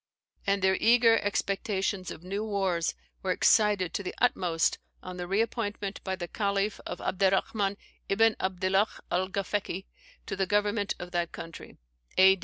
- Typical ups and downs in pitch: No, narrow, 1.9 semitones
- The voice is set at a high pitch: Yes, high, 195 Hz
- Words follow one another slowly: No, average, 150 wpm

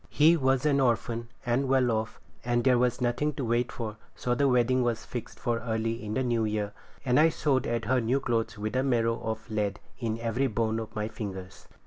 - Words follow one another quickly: Yes, fast, 215 wpm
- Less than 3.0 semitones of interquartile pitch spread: Yes, narrow, 2.5 semitones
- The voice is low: Yes, low, 120 Hz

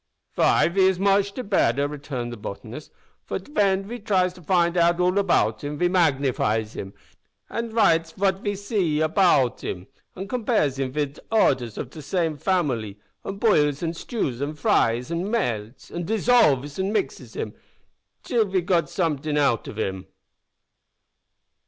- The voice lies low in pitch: No, medium, 170 Hz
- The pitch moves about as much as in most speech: No, wide, 6.0 semitones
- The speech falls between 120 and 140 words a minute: No, average, 160 wpm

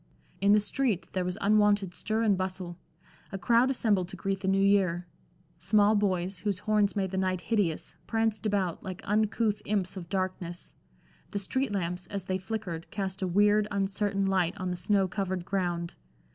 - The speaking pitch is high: Yes, high, 195 Hz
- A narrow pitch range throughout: Yes, narrow, 2.1 semitones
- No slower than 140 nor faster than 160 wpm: No, average, 175 wpm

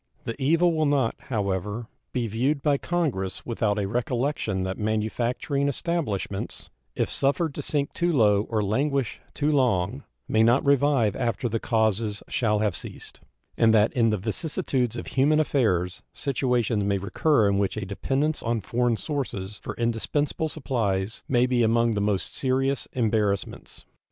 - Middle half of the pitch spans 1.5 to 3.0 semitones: No, average, 4.9 semitones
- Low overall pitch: Yes, low, 115 Hz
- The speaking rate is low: No, average, 155 wpm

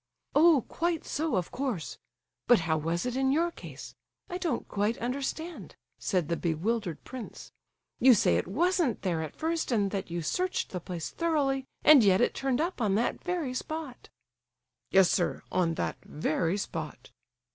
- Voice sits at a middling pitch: No, high, 240 Hz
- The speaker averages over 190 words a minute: No, average, 160 wpm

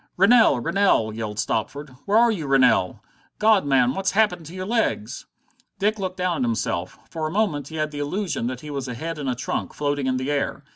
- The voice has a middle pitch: Yes, medium, 150 Hz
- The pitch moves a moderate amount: No, wide, 6.9 semitones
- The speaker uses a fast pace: Yes, fast, 220 wpm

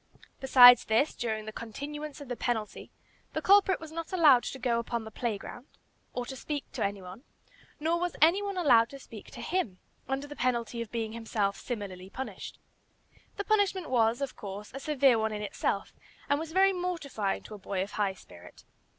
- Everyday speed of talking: Yes, average, 195 wpm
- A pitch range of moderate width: No, wide, 5.8 semitones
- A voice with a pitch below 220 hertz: No, high, 245 Hz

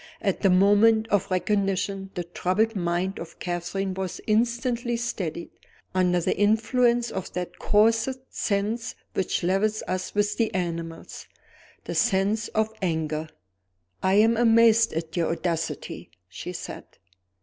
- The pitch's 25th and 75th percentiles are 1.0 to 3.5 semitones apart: No, average, 3.9 semitones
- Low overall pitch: No, high, 195 Hz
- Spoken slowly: Yes, slow, 130 wpm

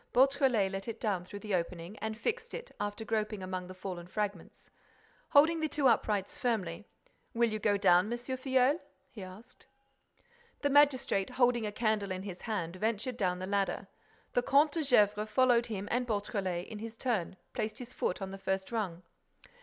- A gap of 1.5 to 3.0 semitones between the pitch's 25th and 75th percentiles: No, average, 4.3 semitones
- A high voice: Yes, high, 215 Hz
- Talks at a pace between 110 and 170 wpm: No, average, 180 wpm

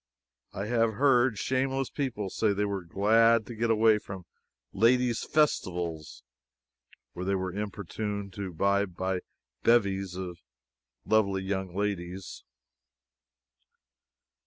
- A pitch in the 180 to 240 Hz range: No, low, 100 Hz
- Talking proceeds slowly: Yes, slow, 110 wpm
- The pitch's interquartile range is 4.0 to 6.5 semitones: No, average, 3.3 semitones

